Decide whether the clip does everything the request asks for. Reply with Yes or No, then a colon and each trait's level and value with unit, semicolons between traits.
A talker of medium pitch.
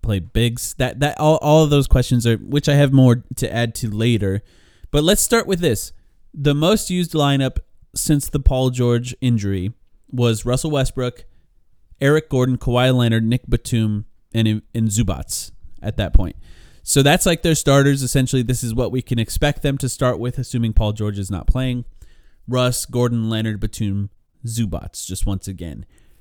No: low, 120 Hz